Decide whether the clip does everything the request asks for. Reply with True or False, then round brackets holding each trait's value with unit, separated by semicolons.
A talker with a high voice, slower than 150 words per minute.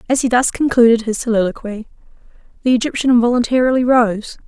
True (235 Hz; 135 wpm)